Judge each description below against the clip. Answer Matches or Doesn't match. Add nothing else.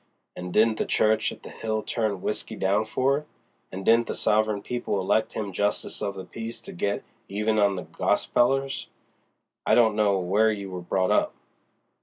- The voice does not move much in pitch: Matches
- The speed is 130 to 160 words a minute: Doesn't match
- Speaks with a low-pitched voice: Matches